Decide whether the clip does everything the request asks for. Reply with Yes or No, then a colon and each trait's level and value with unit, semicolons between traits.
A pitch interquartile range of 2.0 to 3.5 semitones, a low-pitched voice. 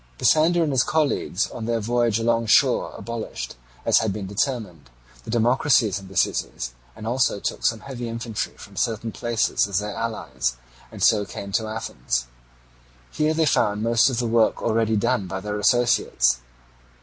Yes: average, 2.8 semitones; low, 110 Hz